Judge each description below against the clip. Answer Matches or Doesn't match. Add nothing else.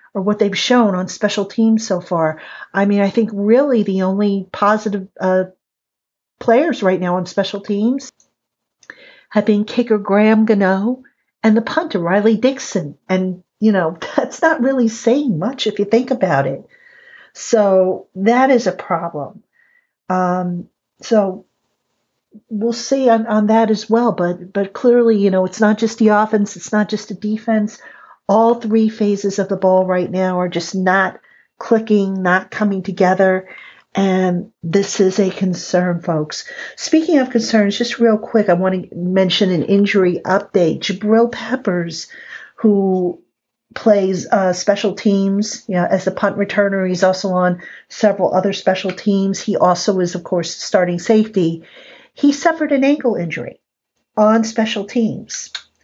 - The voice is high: Matches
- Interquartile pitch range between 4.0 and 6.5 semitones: Doesn't match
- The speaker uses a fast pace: Doesn't match